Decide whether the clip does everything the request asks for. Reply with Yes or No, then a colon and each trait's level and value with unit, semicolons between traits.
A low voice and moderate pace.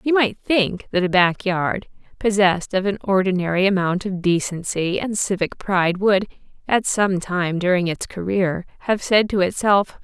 No: high, 190 Hz; average, 165 wpm